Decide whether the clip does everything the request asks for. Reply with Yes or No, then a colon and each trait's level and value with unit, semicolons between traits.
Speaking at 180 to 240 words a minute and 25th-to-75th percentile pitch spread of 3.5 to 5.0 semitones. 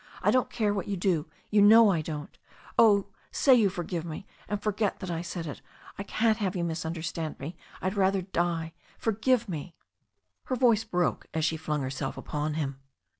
Yes: average, 190 wpm; average, 4.5 semitones